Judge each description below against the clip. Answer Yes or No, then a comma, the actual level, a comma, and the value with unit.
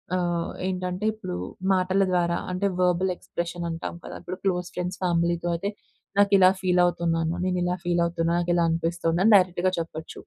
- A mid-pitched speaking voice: Yes, medium, 175 Hz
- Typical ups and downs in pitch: No, narrow, 1.3 semitones